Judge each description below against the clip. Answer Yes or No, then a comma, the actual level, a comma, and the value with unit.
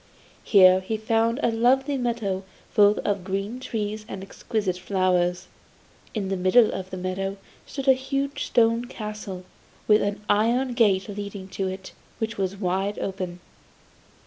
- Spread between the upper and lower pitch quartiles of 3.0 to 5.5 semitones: Yes, average, 3.4 semitones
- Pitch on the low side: No, high, 205 Hz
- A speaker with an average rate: Yes, average, 145 wpm